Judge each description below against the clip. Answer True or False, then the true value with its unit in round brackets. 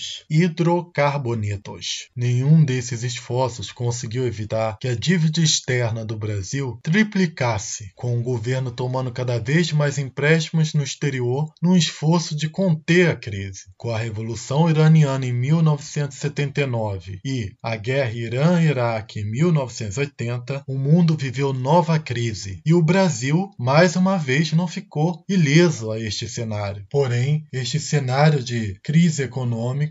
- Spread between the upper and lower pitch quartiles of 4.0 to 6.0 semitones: True (5.1 semitones)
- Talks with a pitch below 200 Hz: True (135 Hz)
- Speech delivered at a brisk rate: False (130 wpm)